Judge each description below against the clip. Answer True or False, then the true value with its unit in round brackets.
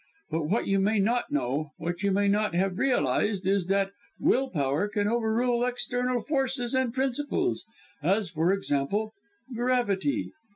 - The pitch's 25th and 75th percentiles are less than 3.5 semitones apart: False (4.6 semitones)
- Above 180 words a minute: False (155 wpm)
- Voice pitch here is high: True (205 Hz)